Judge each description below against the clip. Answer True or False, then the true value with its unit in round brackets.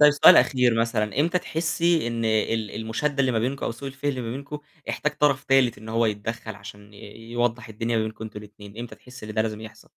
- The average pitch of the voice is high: False (115 Hz)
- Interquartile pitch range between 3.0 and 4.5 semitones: True (3.6 semitones)